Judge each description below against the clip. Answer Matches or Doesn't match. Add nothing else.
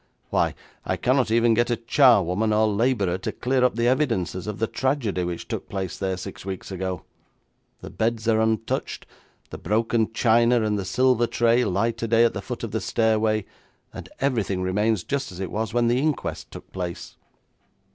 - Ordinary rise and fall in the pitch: Matches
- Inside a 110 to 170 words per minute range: Doesn't match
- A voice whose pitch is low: Matches